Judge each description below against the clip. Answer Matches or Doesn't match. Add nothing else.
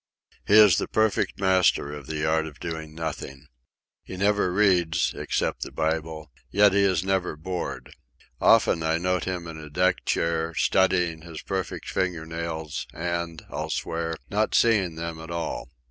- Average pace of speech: Matches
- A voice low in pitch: Matches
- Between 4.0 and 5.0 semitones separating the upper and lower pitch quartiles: Doesn't match